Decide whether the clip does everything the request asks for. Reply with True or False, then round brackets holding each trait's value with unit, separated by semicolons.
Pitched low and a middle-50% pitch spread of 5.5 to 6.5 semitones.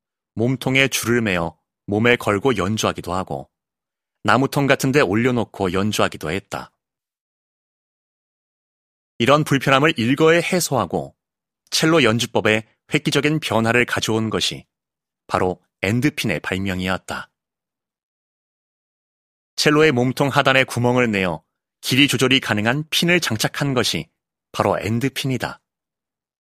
False (120 Hz; 5.1 semitones)